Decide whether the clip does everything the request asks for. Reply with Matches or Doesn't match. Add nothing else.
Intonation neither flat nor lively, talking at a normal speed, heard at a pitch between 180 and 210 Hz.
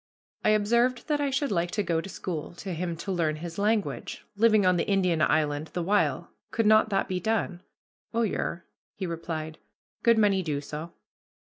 Matches